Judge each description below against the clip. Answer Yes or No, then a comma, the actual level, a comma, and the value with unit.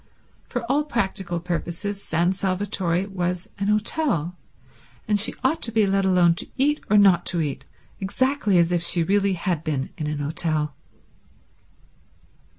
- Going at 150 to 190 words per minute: Yes, average, 155 wpm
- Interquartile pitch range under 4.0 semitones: Yes, average, 3.4 semitones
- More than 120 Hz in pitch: Yes, medium, 185 Hz